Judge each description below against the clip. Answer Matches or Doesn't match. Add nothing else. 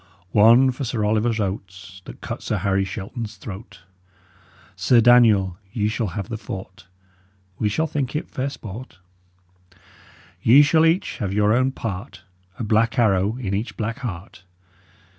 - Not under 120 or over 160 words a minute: Matches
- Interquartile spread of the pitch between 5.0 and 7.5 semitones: Doesn't match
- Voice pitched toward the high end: Doesn't match